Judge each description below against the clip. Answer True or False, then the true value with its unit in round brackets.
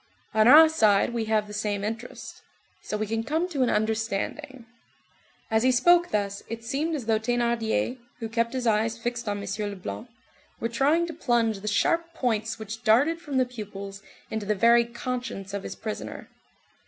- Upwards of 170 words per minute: True (180 wpm)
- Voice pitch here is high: True (230 Hz)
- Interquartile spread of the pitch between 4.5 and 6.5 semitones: False (3.1 semitones)